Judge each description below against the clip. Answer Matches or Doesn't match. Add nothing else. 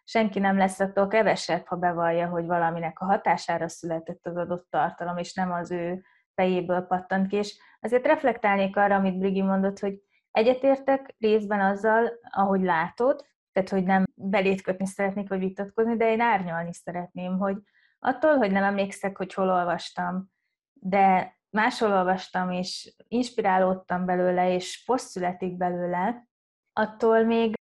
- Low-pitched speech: Doesn't match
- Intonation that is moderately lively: Matches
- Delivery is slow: Doesn't match